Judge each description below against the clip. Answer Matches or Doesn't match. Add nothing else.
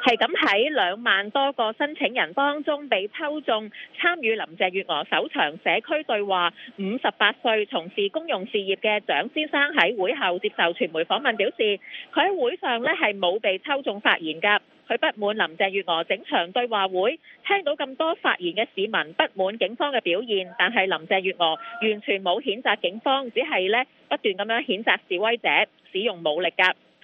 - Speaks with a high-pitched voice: Matches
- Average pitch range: Doesn't match